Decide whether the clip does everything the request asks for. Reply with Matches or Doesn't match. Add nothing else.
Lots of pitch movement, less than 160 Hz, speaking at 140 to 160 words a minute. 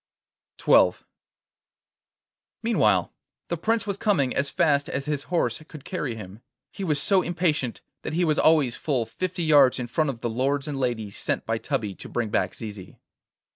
Doesn't match